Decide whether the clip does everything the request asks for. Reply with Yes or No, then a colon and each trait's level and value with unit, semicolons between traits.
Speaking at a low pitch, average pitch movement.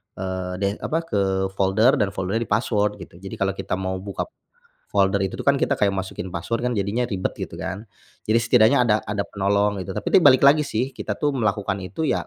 Yes: low, 100 Hz; average, 3.4 semitones